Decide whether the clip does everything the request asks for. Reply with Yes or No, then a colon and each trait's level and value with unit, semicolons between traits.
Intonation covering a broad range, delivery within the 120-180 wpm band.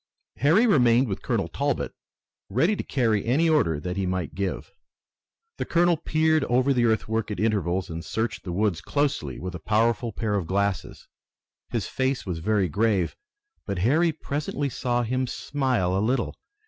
Yes: wide, 6.0 semitones; average, 165 wpm